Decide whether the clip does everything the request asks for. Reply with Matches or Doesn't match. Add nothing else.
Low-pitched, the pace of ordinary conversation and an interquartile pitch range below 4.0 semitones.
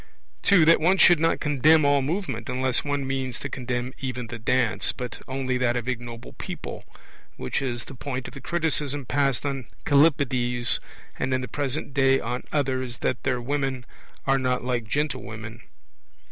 Matches